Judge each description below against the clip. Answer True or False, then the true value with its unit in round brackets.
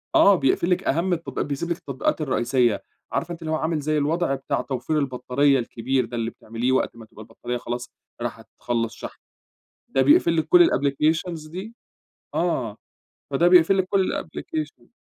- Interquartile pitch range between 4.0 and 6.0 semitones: True (5.2 semitones)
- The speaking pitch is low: False (145 Hz)